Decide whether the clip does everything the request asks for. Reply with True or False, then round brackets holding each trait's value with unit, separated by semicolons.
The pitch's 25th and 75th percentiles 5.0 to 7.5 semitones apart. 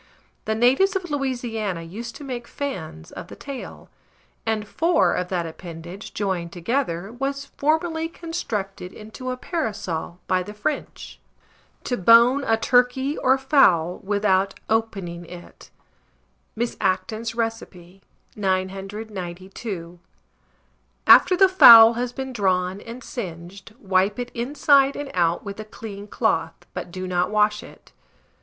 True (5.5 semitones)